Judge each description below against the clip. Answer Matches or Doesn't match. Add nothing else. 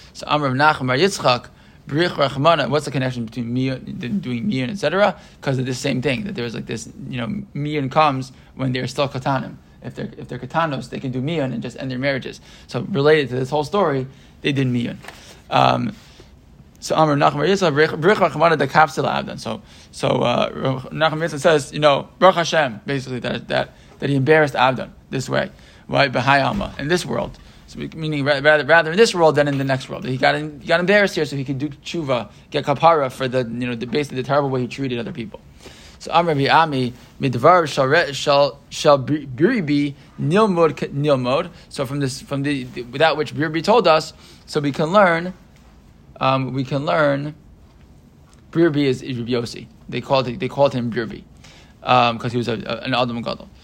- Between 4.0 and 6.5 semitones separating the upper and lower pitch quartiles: Doesn't match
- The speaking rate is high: Doesn't match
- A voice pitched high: Doesn't match